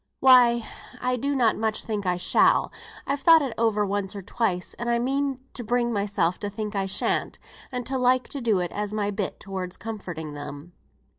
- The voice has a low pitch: No, high, 215 Hz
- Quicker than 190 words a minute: Yes, average, 200 wpm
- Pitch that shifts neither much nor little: Yes, average, 4.2 semitones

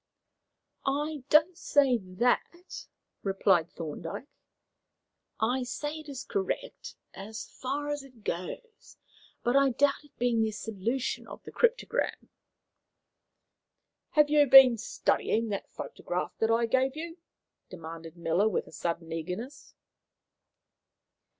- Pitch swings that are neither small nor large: No, wide, 7.0 semitones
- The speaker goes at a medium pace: No, slow, 115 wpm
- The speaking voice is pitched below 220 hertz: No, high, 245 Hz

